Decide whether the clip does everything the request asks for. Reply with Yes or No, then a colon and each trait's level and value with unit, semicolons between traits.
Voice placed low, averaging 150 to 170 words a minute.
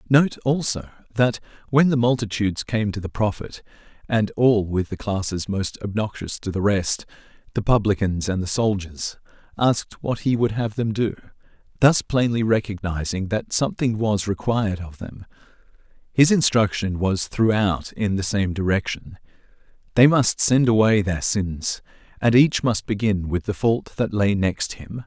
Yes: low, 105 Hz; average, 155 wpm